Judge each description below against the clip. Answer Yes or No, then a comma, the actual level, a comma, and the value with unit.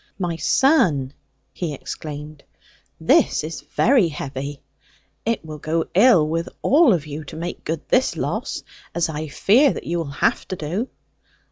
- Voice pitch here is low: No, medium, 165 Hz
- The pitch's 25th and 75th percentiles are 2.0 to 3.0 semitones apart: No, average, 4.5 semitones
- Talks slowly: No, average, 155 wpm